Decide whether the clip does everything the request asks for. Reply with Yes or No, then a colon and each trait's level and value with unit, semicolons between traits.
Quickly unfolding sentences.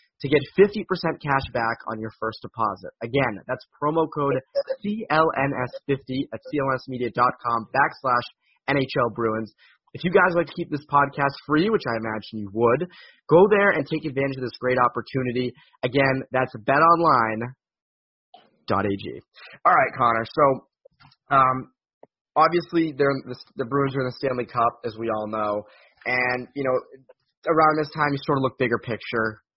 No: average, 155 wpm